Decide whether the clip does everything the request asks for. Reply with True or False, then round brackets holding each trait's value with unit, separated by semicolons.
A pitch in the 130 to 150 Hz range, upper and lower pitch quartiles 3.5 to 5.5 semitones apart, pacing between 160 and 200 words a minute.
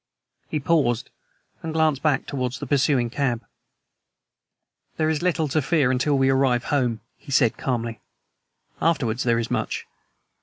False (135 Hz; 3.9 semitones; 145 wpm)